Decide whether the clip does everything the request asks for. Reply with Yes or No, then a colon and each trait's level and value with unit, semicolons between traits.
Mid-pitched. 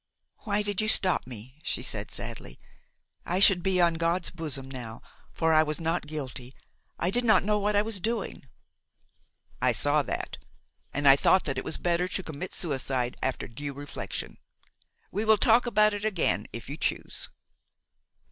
Yes: medium, 170 Hz